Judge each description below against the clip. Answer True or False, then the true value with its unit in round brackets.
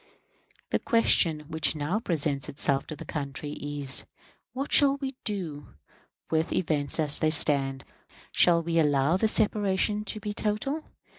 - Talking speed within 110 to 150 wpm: True (145 wpm)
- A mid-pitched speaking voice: True (160 Hz)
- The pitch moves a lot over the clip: True (6.3 semitones)